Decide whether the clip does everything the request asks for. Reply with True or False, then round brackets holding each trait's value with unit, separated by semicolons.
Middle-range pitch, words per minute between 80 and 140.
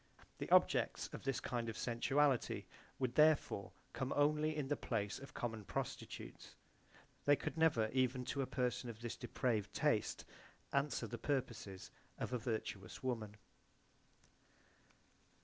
False (125 Hz; 135 wpm)